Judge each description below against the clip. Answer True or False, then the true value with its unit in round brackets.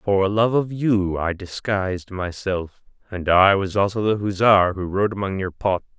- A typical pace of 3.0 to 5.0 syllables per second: True (4.4 syllables/s)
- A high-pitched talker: False (100 Hz)